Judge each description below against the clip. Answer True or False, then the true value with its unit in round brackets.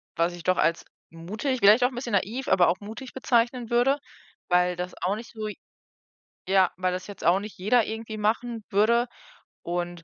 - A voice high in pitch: True (210 Hz)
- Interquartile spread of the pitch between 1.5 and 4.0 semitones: False (4.8 semitones)